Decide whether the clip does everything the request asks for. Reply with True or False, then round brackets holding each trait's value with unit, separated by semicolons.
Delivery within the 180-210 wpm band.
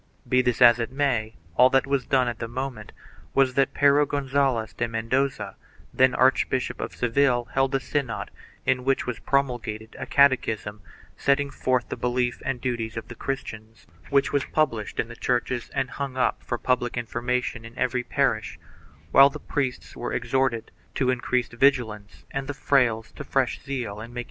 True (185 wpm)